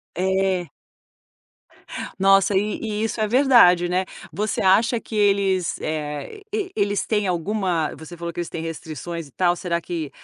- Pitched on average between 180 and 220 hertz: Yes, medium, 185 Hz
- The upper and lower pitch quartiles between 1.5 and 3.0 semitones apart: No, average, 3.4 semitones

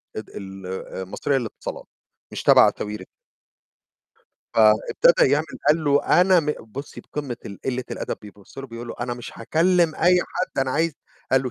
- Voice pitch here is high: No, low, 135 Hz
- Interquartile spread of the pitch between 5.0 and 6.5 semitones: Yes, wide, 5.4 semitones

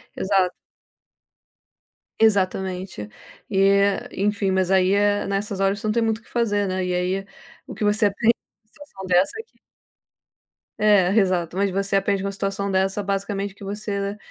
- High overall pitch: Yes, high, 195 Hz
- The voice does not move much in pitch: Yes, narrow, 1.3 semitones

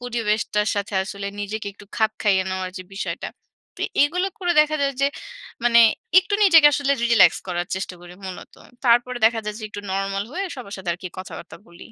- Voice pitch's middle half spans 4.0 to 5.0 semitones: Yes, average, 4.7 semitones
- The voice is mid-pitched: No, high, 210 Hz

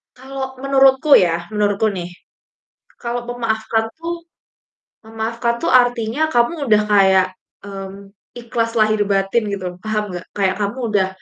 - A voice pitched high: Yes, high, 220 Hz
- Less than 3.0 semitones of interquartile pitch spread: No, average, 3.6 semitones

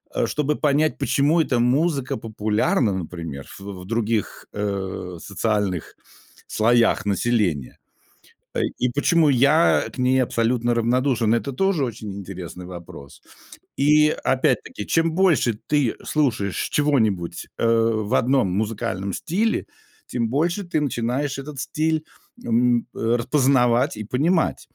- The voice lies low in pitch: Yes, low, 120 Hz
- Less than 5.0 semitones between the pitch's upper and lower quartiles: No, wide, 5.6 semitones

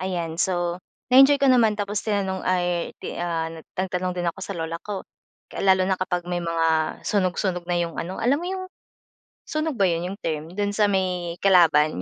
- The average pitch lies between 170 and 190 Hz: Yes, medium, 185 Hz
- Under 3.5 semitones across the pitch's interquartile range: Yes, average, 2.9 semitones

